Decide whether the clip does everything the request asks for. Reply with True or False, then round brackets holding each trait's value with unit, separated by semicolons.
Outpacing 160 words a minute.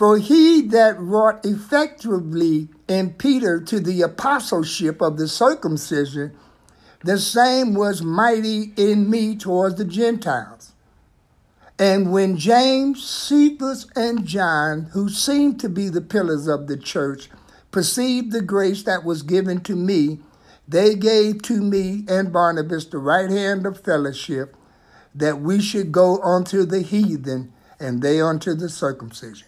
False (140 wpm)